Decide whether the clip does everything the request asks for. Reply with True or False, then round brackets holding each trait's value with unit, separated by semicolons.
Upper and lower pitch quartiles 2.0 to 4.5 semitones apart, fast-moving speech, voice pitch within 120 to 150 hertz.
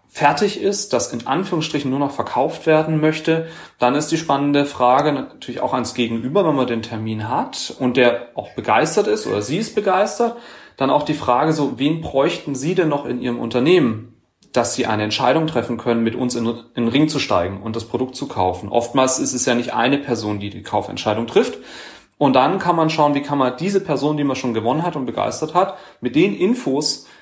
False (4.9 semitones; 210 wpm; 135 Hz)